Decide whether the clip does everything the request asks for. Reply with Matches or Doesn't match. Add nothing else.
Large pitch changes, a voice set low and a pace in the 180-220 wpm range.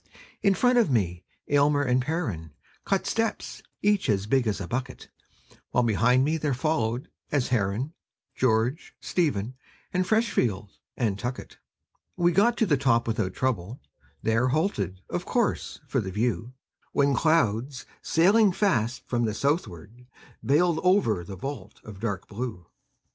Doesn't match